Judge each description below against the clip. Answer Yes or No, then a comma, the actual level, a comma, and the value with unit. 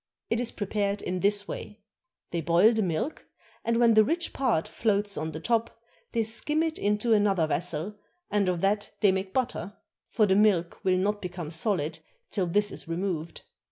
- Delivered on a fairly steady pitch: No, average, 3.6 semitones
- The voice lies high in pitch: Yes, high, 205 Hz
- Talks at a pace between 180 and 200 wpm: Yes, average, 185 wpm